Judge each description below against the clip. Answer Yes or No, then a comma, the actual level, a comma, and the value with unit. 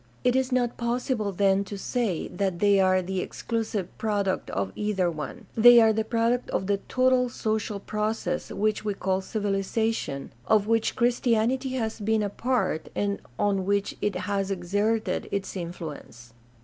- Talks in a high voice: Yes, high, 210 Hz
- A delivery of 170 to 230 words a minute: No, average, 160 wpm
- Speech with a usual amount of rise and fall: Yes, average, 3.0 semitones